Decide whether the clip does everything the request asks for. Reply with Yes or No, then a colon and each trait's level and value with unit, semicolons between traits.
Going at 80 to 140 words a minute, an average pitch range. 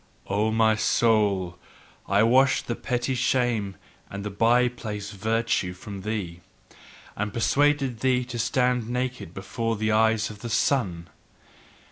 Yes: slow, 135 wpm; average, 3.2 semitones